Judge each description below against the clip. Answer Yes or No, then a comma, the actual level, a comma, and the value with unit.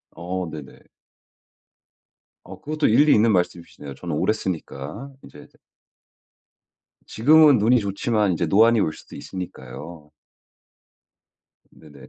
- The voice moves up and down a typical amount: No, wide, 6.3 semitones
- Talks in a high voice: No, very low, 95 Hz